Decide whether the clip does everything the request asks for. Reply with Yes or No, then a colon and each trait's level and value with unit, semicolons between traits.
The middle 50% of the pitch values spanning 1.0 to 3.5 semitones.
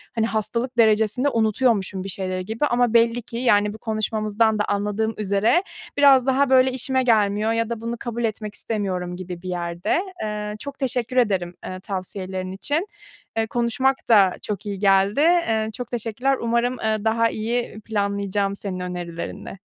Yes: average, 3.2 semitones